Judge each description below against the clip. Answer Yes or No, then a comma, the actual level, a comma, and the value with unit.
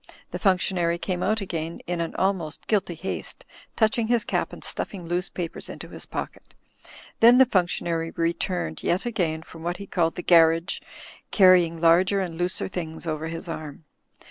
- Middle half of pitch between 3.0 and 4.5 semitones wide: No, narrow, 2.5 semitones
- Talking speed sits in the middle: Yes, average, 170 wpm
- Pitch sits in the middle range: Yes, medium, 175 Hz